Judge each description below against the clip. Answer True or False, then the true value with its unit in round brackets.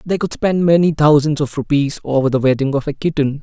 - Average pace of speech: False (230 wpm)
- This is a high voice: False (150 Hz)